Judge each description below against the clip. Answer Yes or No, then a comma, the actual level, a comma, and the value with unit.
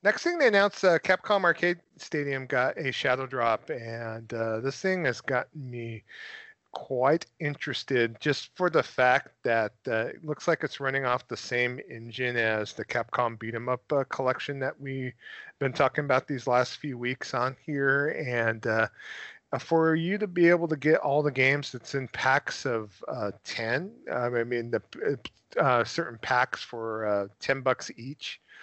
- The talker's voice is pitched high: No, low, 130 Hz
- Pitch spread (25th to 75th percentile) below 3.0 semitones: No, average, 3.9 semitones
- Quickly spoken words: No, average, 175 wpm